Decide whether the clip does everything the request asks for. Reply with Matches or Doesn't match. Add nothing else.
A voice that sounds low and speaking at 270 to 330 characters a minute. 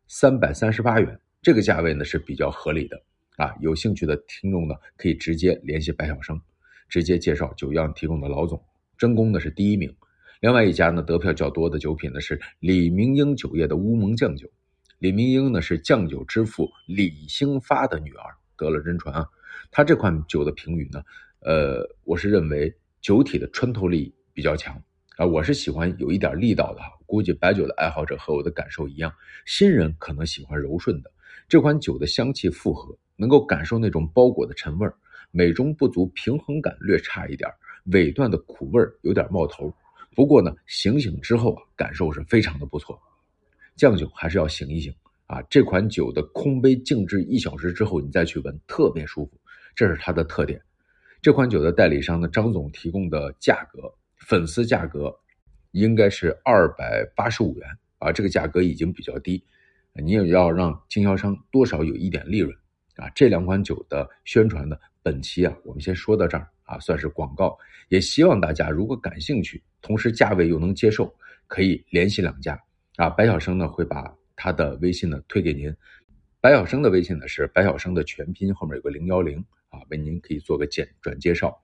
Matches